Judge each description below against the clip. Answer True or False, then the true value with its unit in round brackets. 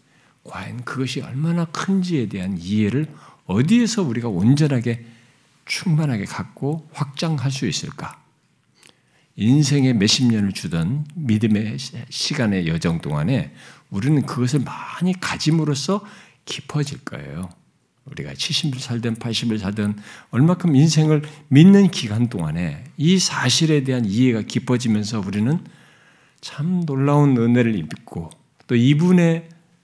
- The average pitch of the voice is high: False (140 Hz)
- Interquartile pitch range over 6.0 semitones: False (5.2 semitones)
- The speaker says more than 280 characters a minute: False (265 characters per minute)